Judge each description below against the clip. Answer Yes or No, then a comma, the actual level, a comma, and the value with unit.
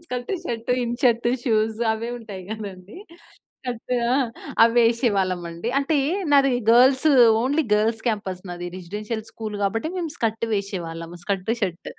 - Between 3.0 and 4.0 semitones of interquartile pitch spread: Yes, average, 3.5 semitones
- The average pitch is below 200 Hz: No, high, 220 Hz